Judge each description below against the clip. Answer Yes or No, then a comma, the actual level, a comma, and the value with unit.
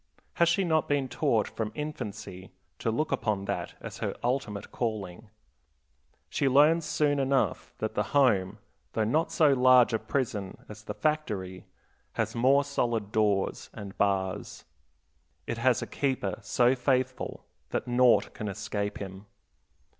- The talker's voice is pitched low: Yes, low, 120 Hz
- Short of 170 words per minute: Yes, average, 145 wpm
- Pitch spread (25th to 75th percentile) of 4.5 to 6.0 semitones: Yes, average, 5.2 semitones